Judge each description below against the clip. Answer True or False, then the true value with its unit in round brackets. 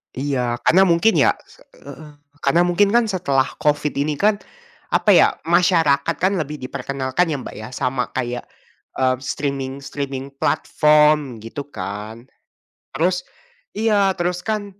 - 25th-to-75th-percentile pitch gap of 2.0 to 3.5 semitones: False (5.2 semitones)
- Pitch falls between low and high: True (150 Hz)